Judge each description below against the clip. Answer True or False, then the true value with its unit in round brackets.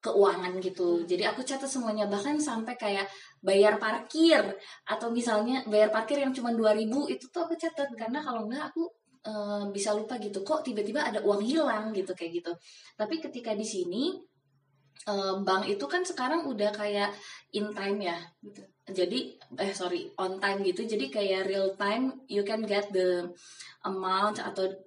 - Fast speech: True (165 wpm)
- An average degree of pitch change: True (4.5 semitones)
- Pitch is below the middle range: False (210 Hz)